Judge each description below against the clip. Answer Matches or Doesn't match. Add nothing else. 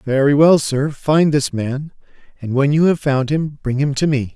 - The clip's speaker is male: Matches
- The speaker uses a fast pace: Matches